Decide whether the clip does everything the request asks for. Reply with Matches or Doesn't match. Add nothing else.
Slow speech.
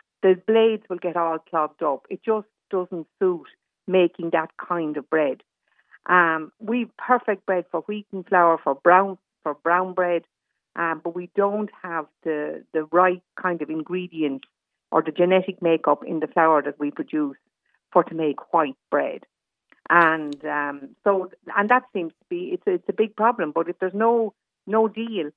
Doesn't match